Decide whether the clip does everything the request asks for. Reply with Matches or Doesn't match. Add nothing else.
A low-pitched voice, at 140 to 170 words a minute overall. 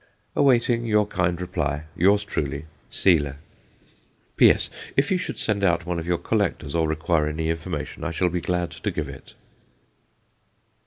Matches